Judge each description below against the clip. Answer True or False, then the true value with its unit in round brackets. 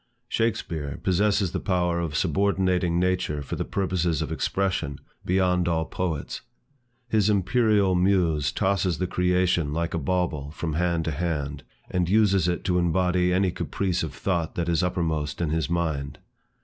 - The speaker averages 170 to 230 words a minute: False (160 wpm)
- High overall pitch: False (90 Hz)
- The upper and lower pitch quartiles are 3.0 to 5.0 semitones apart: False (2.4 semitones)